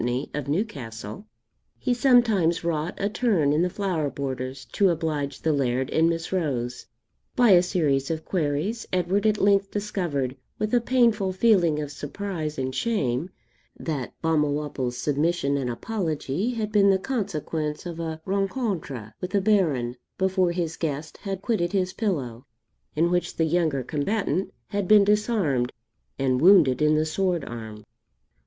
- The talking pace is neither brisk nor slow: Yes, average, 150 wpm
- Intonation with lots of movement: Yes, wide, 5.8 semitones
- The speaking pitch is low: No, medium, 165 Hz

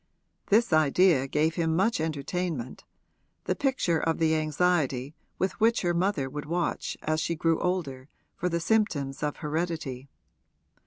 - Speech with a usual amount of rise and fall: Yes, average, 3.3 semitones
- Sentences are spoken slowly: No, average, 145 wpm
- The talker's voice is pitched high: No, medium, 160 Hz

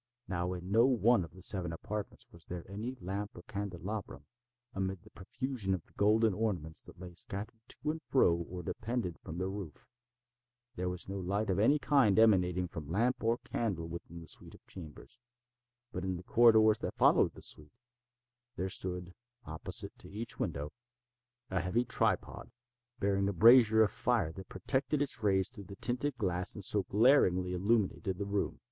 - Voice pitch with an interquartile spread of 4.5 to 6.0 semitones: No, average, 3.9 semitones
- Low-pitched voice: Yes, low, 100 Hz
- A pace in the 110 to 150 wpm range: No, average, 175 wpm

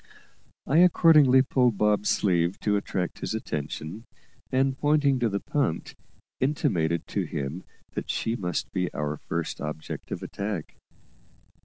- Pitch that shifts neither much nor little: No, wide, 7.6 semitones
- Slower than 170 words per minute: Yes, slow, 135 wpm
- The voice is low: Yes, low, 105 Hz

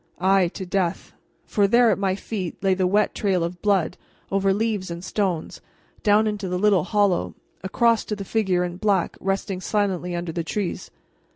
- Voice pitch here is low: No, high, 195 Hz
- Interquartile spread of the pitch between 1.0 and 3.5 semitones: Yes, narrow, 2.4 semitones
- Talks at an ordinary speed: Yes, average, 180 wpm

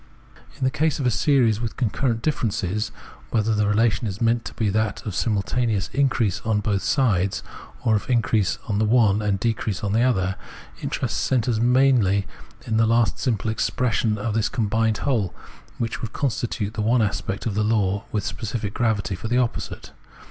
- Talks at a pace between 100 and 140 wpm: No, average, 185 wpm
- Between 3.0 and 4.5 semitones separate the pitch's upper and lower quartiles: No, narrow, 2.5 semitones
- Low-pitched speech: Yes, low, 110 Hz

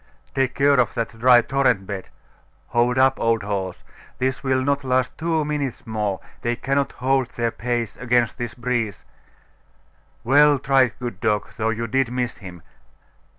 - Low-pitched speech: Yes, low, 125 Hz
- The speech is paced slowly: No, average, 155 wpm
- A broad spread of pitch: No, average, 2.7 semitones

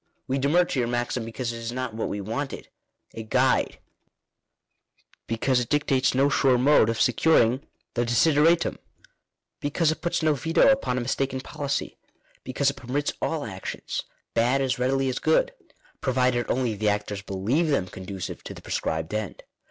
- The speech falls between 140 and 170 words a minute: Yes, average, 165 wpm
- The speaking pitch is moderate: No, low, 130 Hz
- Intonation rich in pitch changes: No, average, 3.7 semitones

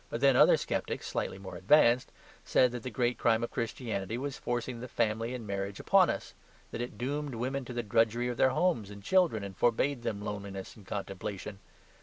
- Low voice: Yes, low, 115 Hz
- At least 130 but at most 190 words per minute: No, average, 200 wpm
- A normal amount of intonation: Yes, average, 3.7 semitones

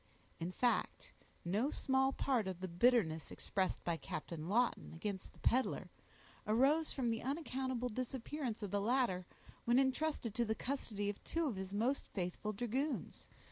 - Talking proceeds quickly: No, average, 155 wpm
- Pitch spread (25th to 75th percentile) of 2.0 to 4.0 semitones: No, average, 5.1 semitones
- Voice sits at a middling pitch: No, high, 235 Hz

